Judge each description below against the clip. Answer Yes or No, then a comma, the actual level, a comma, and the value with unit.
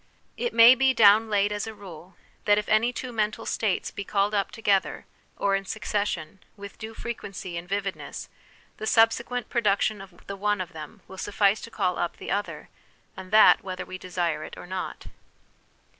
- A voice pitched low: No, high, 200 Hz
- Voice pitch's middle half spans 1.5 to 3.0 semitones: Yes, average, 2.7 semitones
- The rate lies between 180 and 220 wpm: Yes, average, 185 wpm